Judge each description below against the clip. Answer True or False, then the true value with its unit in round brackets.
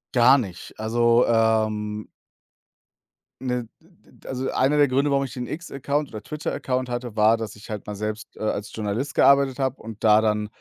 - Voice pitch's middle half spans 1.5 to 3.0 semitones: False (3.6 semitones)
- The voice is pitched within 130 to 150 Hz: False (120 Hz)